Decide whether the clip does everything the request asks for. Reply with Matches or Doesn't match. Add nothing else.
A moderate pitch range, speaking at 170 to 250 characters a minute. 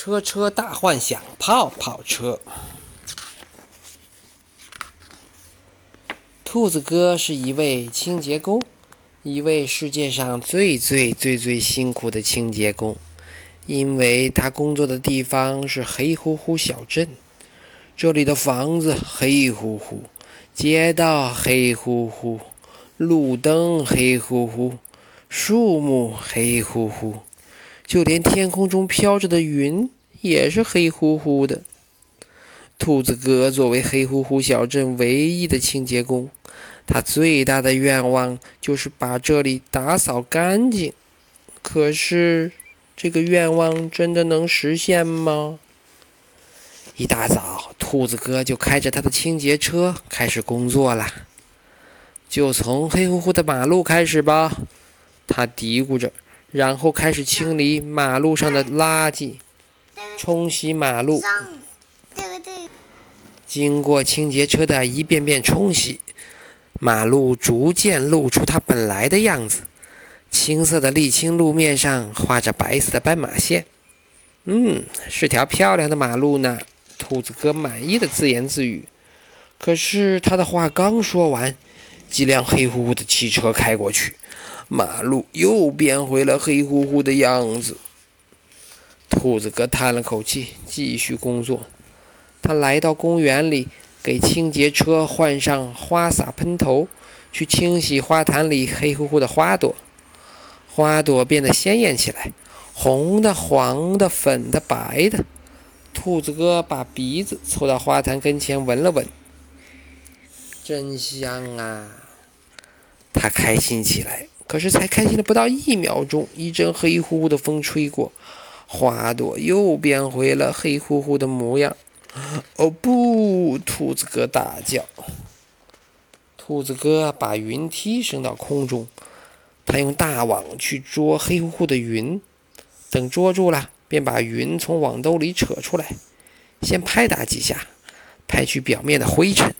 Matches